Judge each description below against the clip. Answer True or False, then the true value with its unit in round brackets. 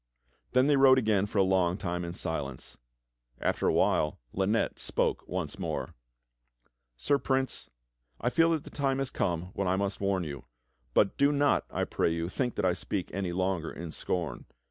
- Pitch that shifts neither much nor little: False (6.9 semitones)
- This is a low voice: True (95 Hz)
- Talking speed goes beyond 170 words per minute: True (185 wpm)